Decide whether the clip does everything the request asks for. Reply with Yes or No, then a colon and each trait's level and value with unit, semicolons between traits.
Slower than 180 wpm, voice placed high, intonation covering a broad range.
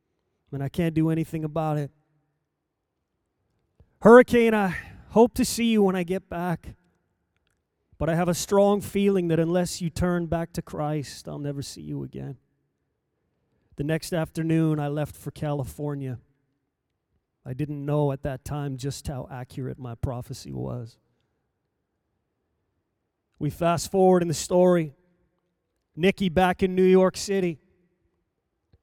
No: average, 140 wpm; medium, 150 Hz; wide, 6.0 semitones